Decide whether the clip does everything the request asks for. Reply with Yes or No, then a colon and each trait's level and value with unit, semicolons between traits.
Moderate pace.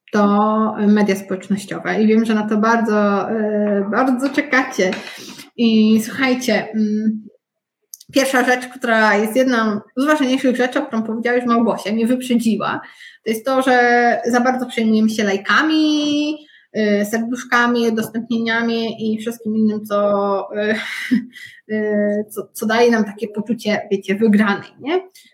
Yes: average, 135 wpm